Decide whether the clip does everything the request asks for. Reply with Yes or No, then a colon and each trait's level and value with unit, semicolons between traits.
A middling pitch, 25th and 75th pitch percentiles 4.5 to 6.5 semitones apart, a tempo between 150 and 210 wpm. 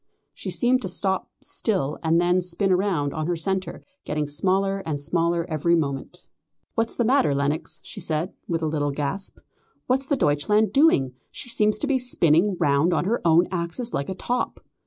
Yes: medium, 175 Hz; average, 5.2 semitones; average, 180 wpm